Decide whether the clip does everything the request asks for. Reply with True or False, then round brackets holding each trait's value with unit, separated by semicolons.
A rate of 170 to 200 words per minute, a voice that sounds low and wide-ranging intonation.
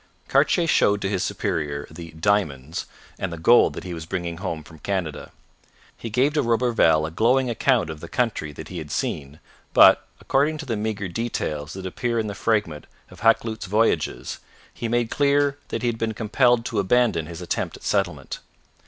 True (190 wpm; 105 Hz; 6.4 semitones)